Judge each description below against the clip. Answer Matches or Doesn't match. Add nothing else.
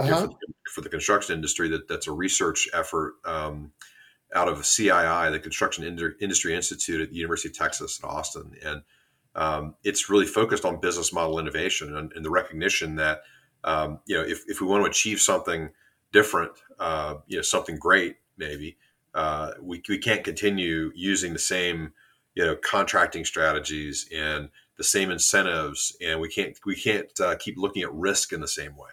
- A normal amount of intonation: Doesn't match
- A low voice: Matches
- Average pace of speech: Matches